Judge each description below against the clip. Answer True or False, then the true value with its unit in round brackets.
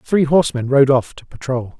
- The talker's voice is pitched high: False (135 Hz)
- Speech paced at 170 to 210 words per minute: True (200 wpm)